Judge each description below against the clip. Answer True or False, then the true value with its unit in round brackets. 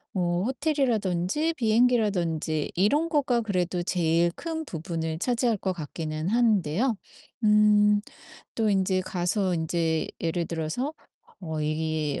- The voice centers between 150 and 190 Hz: True (185 Hz)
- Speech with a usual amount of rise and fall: False (5.9 semitones)